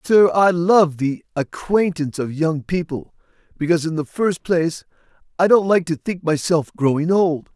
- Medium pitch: Yes, medium, 165 Hz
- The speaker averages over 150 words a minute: Yes, average, 165 wpm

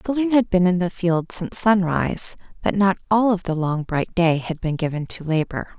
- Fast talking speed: Yes, fast, 230 wpm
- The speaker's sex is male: No, female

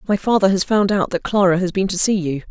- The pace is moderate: No, fast, 285 wpm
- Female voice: Yes, female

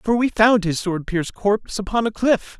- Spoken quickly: Yes, fast, 230 wpm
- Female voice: No, male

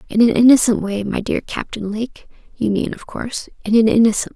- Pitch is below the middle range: No, high, 220 Hz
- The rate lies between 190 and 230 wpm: Yes, fast, 205 wpm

